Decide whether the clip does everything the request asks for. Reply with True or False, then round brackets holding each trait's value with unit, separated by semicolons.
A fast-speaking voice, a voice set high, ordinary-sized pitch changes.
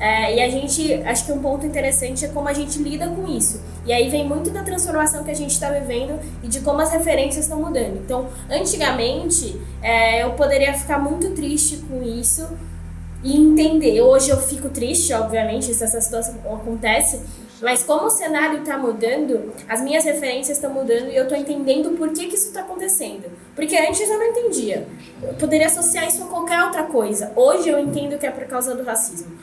True (200 wpm; 285 Hz; 4.6 semitones)